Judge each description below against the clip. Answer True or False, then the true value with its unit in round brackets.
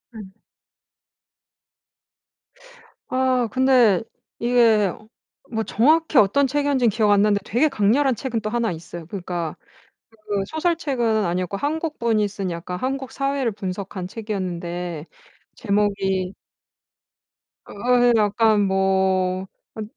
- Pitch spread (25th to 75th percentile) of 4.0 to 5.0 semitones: True (4.7 semitones)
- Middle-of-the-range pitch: False (215 Hz)